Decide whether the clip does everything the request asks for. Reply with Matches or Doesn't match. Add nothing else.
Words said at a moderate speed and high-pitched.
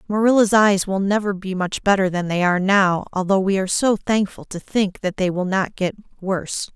Doesn't match